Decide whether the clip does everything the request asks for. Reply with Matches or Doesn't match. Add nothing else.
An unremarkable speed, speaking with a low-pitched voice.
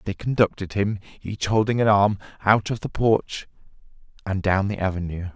Matches